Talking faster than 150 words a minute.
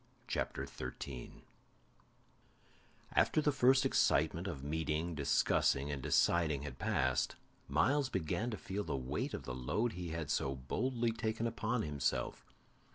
No: slow, 135 wpm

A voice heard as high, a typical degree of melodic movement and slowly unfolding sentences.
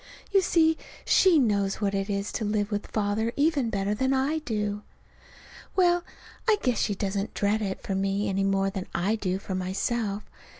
No: high, 205 Hz; average, 4.2 semitones; average, 180 wpm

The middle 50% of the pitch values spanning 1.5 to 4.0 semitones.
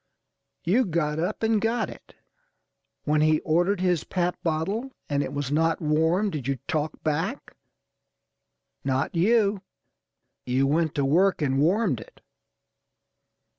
No: average, 4.5 semitones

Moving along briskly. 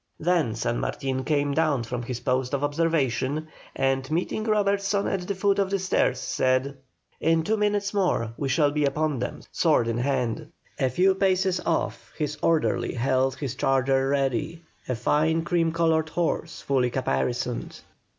No: average, 160 wpm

